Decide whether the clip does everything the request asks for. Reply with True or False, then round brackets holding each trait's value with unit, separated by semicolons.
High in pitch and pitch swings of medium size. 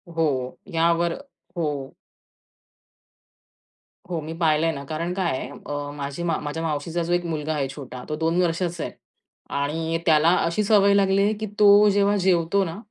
False (165 Hz; 3.0 semitones)